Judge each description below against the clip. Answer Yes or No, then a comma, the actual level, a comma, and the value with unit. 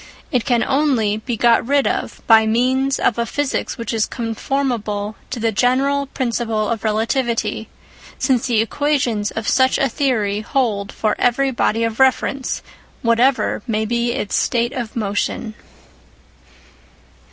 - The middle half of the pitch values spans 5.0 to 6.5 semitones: No, average, 3.2 semitones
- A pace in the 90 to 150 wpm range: Yes, average, 140 wpm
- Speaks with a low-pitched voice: No, high, 235 Hz